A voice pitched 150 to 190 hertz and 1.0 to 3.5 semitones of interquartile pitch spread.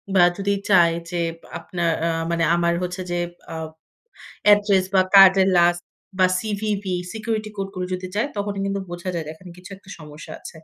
Yes: medium, 185 Hz; narrow, 2.5 semitones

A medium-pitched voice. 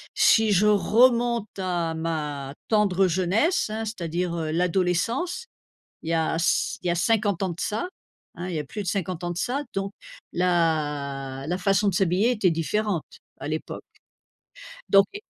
Yes: medium, 180 Hz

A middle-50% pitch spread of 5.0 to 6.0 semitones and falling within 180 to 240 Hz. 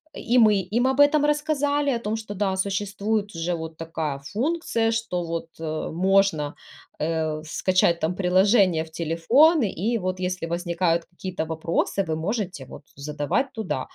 Yes: wide, 5.4 semitones; medium, 185 Hz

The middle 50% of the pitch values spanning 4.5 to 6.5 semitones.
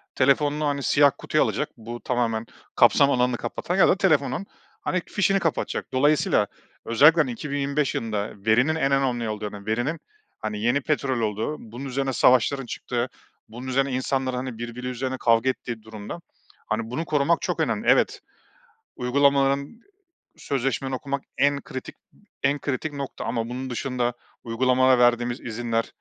No: average, 2.9 semitones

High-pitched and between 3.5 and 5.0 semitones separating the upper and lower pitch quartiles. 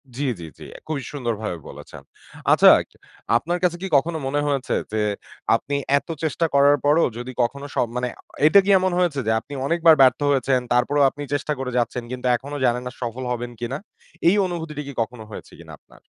No: medium, 140 Hz; average, 3.8 semitones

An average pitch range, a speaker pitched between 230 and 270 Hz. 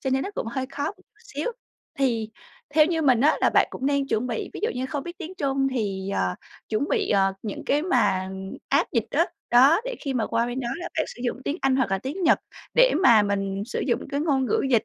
Yes: average, 5.0 semitones; very high, 265 Hz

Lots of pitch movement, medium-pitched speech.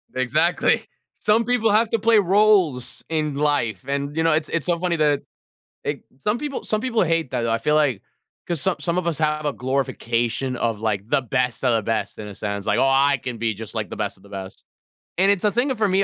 Yes: wide, 7.6 semitones; medium, 150 Hz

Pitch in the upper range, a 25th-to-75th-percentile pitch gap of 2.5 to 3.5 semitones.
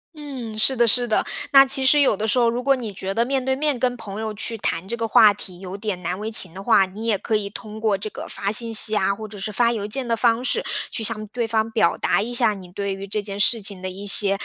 Yes: high, 220 Hz; average, 3.0 semitones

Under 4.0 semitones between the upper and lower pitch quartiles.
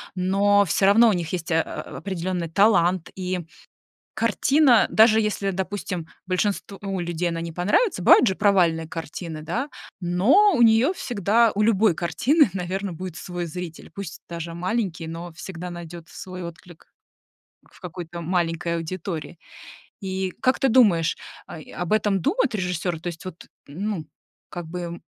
Yes: average, 3.2 semitones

